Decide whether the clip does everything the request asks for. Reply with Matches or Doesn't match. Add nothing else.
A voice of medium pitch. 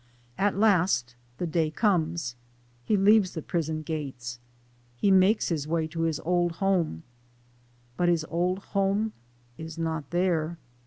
Matches